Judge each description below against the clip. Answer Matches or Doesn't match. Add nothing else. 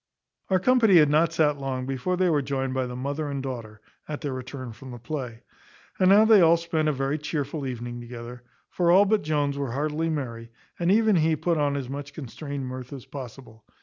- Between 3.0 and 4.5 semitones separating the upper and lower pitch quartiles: Matches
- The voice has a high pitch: Doesn't match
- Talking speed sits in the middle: Doesn't match